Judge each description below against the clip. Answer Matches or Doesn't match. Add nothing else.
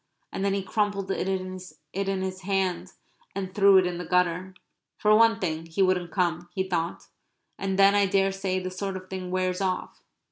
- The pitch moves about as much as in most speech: Doesn't match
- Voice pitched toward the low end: Doesn't match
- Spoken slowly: Doesn't match